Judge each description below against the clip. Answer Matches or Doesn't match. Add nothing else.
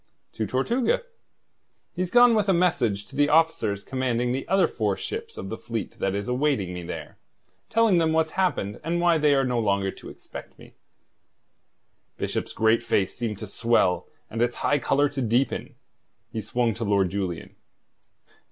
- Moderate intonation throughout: Doesn't match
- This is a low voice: Matches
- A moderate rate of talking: Matches